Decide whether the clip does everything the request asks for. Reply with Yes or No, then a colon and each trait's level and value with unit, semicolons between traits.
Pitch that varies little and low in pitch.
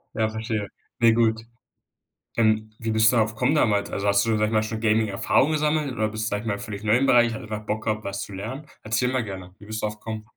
Yes: narrow, 1.4 semitones; low, 110 Hz